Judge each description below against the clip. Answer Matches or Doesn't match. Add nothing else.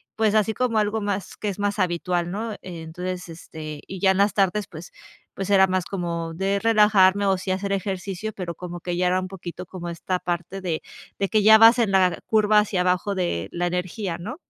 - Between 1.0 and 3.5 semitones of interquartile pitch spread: Matches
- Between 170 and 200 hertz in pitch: Matches